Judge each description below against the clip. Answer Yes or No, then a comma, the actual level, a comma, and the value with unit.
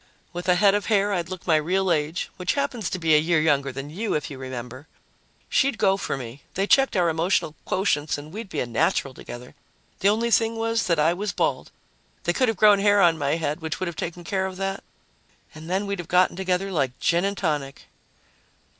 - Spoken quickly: Yes, fast, 225 wpm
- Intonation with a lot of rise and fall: No, average, 4.6 semitones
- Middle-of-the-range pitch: Yes, medium, 175 Hz